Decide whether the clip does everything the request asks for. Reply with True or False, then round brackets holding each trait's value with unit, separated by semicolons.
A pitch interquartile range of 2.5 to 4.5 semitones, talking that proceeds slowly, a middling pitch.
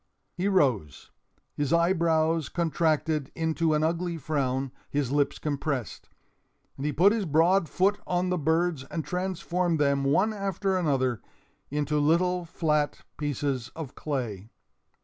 True (3.7 semitones; 130 wpm; 155 Hz)